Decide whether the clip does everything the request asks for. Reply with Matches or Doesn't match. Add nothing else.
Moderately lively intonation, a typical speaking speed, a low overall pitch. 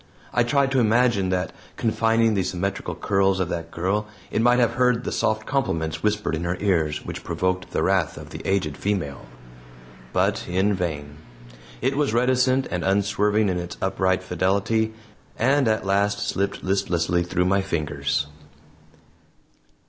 Matches